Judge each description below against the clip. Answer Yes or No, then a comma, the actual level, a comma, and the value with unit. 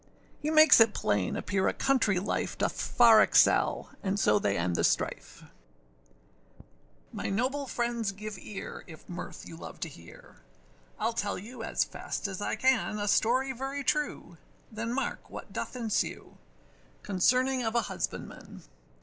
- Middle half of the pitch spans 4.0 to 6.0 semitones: Yes, average, 4.8 semitones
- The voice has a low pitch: No, high, 220 Hz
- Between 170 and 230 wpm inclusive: No, average, 155 wpm